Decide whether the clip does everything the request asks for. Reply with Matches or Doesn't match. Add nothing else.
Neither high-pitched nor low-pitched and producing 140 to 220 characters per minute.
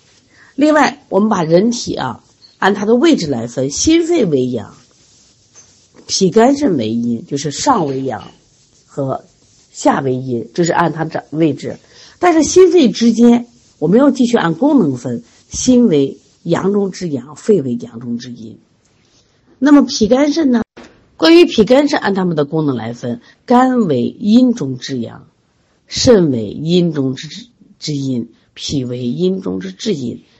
Matches